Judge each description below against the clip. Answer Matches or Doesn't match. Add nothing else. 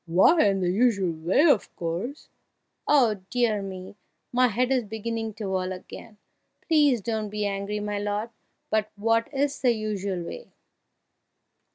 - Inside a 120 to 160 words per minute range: Matches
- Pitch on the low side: Doesn't match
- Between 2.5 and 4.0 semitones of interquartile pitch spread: Matches